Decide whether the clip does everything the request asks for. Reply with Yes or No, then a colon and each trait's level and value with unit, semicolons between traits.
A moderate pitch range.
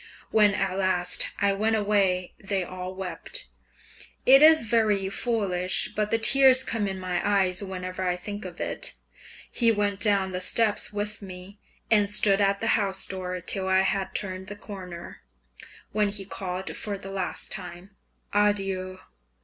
No: narrow, 1.9 semitones